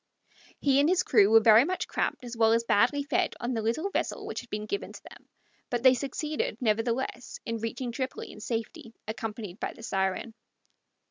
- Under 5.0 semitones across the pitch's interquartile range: Yes, average, 3.3 semitones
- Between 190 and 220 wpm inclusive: Yes, average, 195 wpm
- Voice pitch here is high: Yes, high, 235 Hz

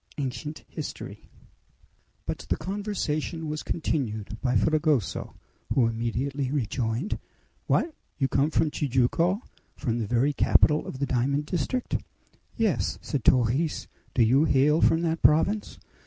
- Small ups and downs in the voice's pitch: No, average, 4.4 semitones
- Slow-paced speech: Yes, slow, 125 wpm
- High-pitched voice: No, medium, 145 Hz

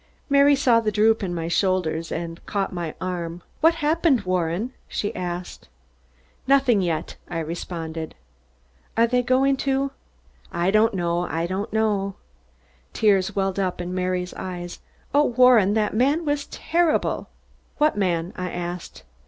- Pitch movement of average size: No, wide, 6.2 semitones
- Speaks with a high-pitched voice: Yes, high, 195 Hz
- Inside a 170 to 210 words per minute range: No, average, 145 wpm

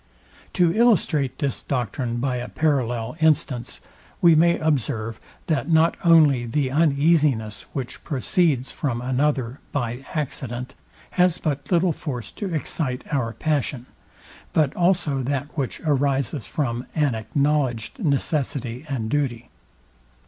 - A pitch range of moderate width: Yes, average, 4.2 semitones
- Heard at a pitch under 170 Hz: Yes, medium, 140 Hz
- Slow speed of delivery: Yes, slow, 120 wpm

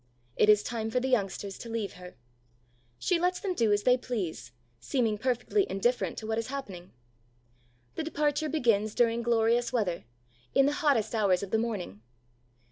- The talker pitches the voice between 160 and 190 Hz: No, high, 230 Hz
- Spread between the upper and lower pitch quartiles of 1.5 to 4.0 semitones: Yes, average, 3.7 semitones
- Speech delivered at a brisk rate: No, average, 170 wpm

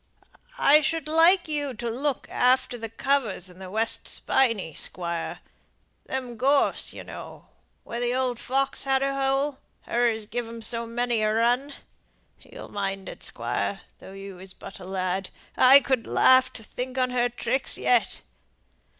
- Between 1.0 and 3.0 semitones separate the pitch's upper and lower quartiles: No, average, 3.8 semitones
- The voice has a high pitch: Yes, high, 245 Hz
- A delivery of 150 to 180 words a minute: Yes, average, 165 wpm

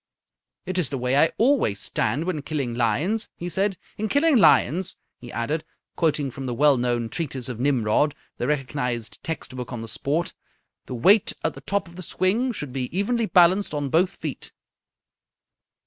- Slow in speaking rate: No, average, 175 wpm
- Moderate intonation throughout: No, wide, 6.7 semitones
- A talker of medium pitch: Yes, medium, 150 Hz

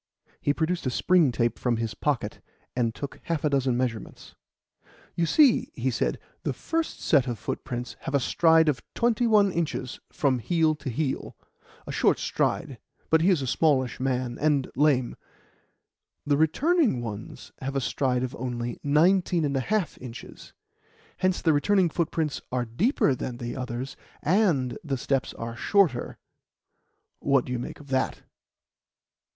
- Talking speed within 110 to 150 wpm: No, average, 160 wpm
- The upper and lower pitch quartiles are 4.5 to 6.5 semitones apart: Yes, average, 4.9 semitones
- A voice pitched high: No, medium, 140 Hz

